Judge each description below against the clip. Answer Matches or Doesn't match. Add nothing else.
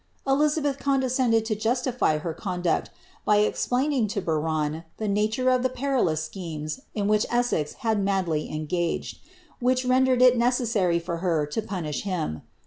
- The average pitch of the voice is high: Matches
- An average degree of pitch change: Doesn't match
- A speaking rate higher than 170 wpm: Doesn't match